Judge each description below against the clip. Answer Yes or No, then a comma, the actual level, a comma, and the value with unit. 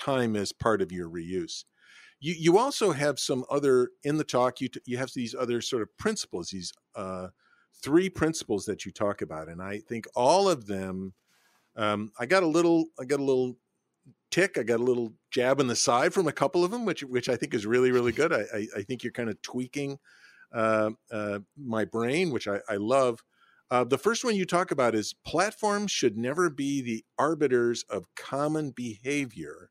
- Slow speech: No, fast, 205 wpm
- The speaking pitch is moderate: No, low, 125 Hz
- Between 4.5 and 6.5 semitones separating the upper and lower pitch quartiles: Yes, average, 5.2 semitones